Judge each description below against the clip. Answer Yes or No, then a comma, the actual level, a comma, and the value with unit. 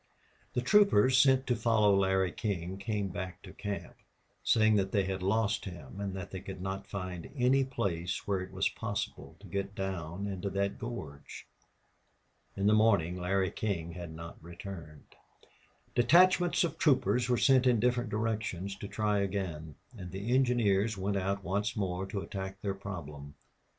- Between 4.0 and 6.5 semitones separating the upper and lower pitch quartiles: No, average, 3.1 semitones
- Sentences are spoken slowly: No, average, 165 wpm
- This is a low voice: Yes, low, 100 Hz